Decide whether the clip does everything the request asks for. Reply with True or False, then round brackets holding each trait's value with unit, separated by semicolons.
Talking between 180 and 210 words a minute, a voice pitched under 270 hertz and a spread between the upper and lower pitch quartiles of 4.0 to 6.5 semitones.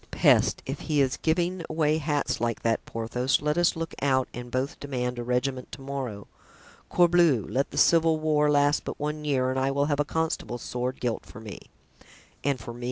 False (200 wpm; 140 Hz; 3.6 semitones)